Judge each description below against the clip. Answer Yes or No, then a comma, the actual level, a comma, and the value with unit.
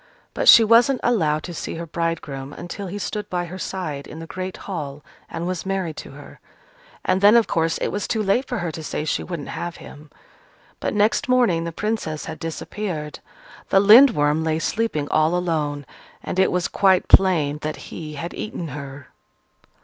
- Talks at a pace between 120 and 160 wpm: No, average, 190 wpm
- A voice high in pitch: No, medium, 170 Hz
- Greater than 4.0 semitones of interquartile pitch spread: Yes, average, 4.6 semitones